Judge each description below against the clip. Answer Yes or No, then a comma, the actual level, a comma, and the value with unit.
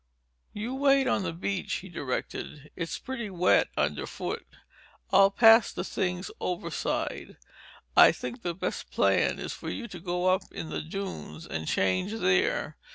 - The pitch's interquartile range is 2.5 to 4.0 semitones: No, average, 4.4 semitones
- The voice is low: No, medium, 185 Hz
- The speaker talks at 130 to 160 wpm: Yes, average, 155 wpm